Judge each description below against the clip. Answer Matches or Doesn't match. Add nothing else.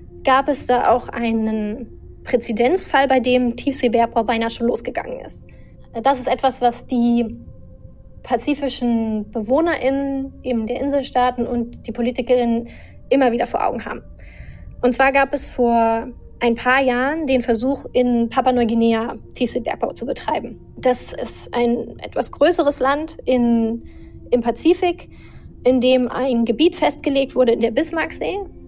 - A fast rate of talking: Doesn't match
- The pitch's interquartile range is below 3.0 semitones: Matches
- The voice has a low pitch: Doesn't match